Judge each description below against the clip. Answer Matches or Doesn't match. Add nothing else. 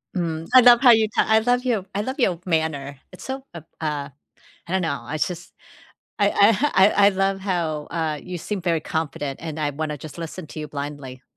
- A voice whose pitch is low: Doesn't match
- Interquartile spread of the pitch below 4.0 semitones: Doesn't match